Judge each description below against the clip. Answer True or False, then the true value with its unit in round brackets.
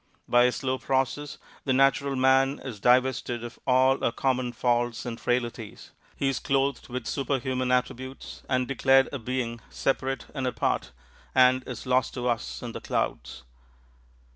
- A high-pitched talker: False (130 Hz)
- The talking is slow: False (155 wpm)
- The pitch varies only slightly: True (1.5 semitones)